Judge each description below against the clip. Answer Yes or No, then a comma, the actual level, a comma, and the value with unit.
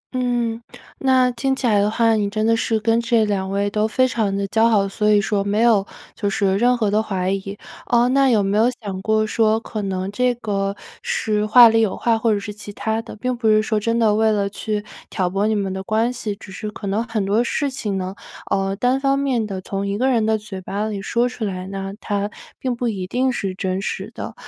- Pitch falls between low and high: No, high, 215 Hz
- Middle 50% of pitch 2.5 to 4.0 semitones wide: Yes, average, 2.8 semitones